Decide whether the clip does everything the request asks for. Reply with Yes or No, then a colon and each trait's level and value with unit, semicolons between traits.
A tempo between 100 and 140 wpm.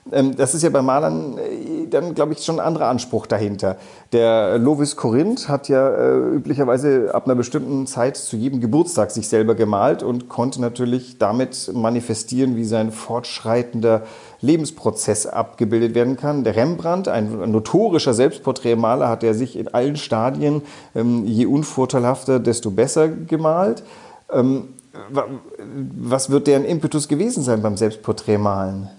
Yes: average, 135 wpm